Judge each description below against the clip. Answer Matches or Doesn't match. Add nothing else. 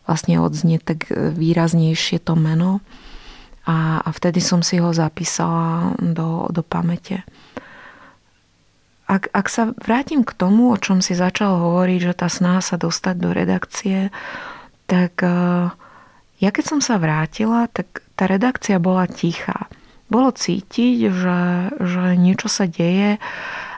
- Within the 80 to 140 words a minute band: Matches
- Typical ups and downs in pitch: Matches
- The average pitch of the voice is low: Doesn't match